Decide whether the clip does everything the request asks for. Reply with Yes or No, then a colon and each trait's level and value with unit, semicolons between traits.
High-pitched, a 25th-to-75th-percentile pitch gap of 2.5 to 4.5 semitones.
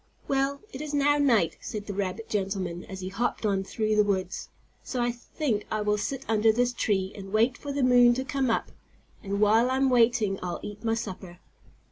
Yes: high, 220 Hz; average, 3.9 semitones